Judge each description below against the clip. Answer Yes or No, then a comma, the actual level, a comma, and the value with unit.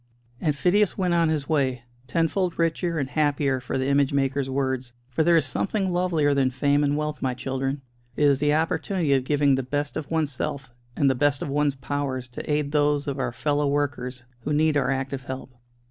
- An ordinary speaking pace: No, fast, 210 wpm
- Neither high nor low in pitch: Yes, medium, 145 Hz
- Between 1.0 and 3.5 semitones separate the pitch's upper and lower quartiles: Yes, narrow, 2.4 semitones